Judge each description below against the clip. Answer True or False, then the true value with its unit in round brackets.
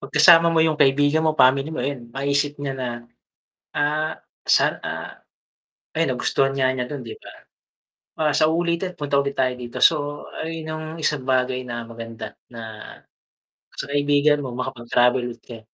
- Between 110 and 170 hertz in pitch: True (140 Hz)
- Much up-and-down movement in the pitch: False (3.2 semitones)